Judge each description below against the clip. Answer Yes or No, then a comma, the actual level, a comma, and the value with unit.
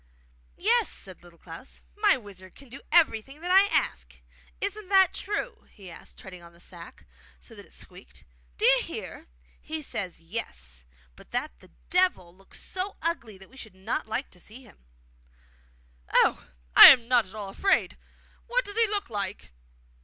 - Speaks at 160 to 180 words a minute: Yes, average, 170 wpm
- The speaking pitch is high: Yes, high, 230 Hz